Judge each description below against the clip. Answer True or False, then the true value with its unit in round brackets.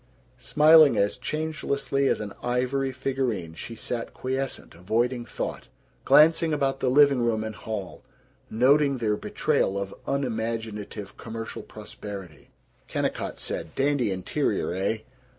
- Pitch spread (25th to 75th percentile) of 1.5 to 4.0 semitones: False (4.4 semitones)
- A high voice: False (120 Hz)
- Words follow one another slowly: True (120 wpm)